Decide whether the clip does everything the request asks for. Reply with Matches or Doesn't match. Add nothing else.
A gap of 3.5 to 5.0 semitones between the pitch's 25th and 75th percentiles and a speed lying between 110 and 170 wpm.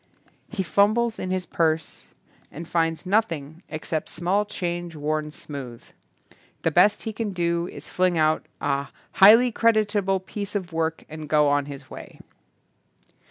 Matches